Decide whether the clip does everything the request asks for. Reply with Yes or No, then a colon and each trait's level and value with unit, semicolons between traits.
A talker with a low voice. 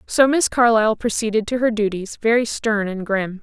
No: high, 220 Hz